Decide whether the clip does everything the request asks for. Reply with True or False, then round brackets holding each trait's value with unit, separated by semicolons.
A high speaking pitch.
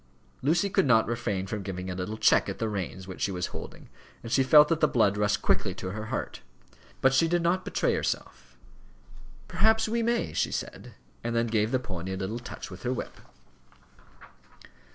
False (115 Hz)